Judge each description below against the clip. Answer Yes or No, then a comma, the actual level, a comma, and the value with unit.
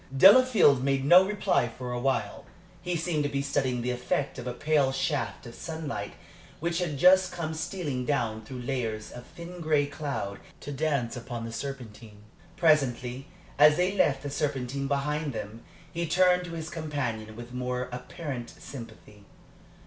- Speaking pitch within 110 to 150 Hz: Yes, medium, 140 Hz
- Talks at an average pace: Yes, average, 165 wpm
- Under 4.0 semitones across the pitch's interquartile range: No, average, 4.4 semitones